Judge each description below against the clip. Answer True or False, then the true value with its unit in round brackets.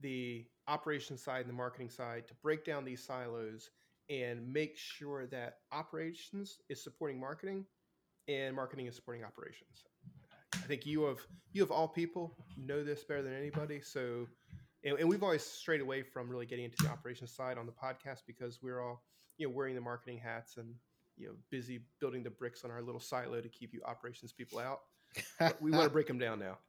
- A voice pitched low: True (130 Hz)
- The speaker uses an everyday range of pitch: True (3.7 semitones)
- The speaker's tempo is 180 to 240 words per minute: True (200 wpm)